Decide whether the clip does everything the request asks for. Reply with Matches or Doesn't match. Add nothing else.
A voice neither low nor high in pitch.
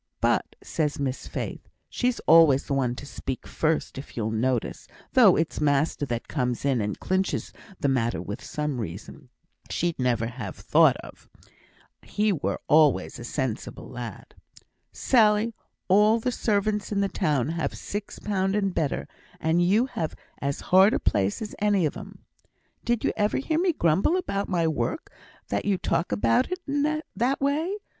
Matches